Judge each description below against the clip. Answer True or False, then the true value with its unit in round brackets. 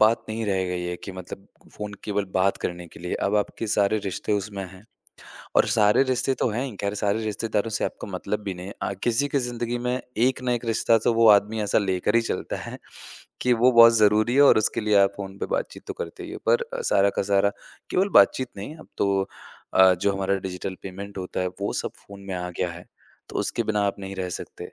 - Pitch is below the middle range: True (105 Hz)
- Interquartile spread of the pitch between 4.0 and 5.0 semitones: False (3.0 semitones)